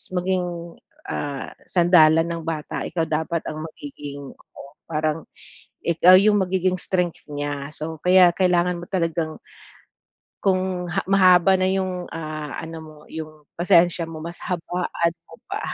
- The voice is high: No, medium, 170 Hz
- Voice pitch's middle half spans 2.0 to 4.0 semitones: Yes, narrow, 2.5 semitones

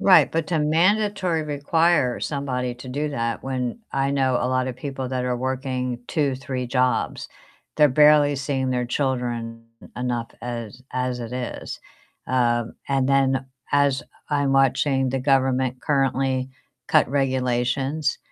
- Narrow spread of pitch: Yes, narrow, 2.1 semitones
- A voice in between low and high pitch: No, low, 130 Hz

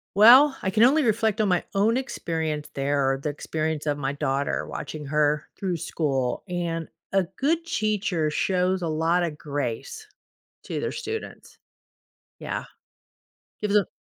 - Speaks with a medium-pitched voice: Yes, medium, 170 Hz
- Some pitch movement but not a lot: No, wide, 6.0 semitones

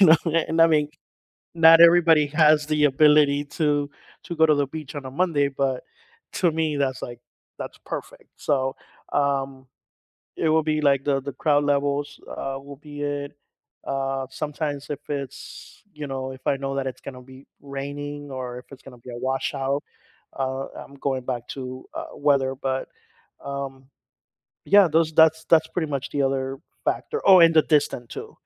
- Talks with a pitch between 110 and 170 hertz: Yes, medium, 140 Hz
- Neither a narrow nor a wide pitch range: No, narrow, 2.2 semitones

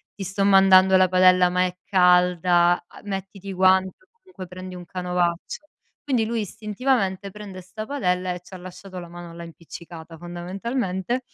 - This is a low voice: No, medium, 185 Hz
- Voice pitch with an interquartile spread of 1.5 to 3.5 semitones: Yes, narrow, 1.8 semitones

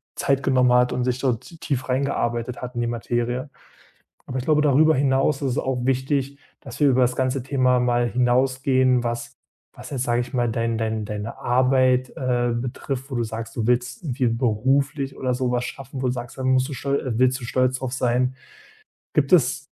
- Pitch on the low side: Yes, low, 125 Hz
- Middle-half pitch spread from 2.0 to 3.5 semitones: No, narrow, 1.6 semitones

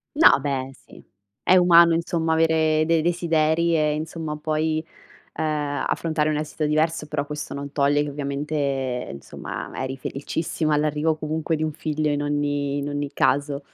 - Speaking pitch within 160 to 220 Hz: No, medium, 150 Hz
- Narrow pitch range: Yes, narrow, 1.8 semitones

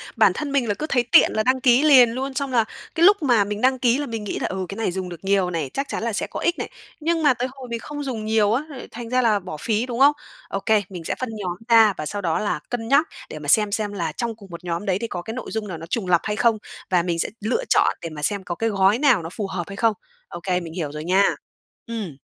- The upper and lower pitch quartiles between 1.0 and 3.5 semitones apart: No, average, 5.3 semitones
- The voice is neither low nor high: No, high, 215 Hz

